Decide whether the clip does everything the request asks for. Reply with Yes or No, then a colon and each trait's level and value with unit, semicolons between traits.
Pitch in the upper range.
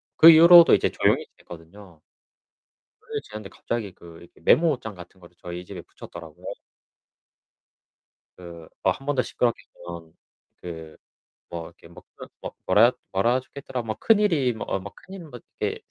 No: low, 100 Hz